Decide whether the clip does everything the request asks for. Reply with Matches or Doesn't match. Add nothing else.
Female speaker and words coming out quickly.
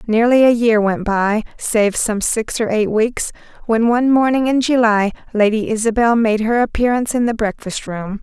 Doesn't match